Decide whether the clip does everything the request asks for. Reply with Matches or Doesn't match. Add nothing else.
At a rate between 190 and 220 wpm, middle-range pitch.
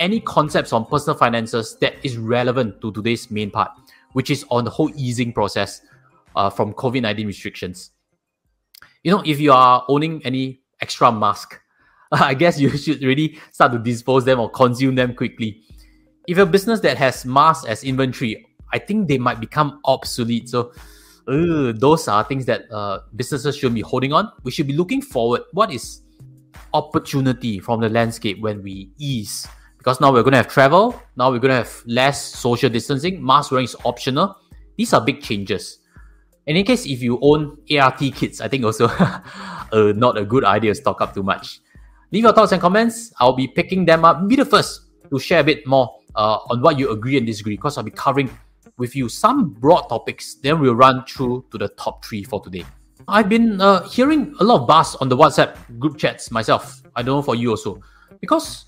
Doesn't match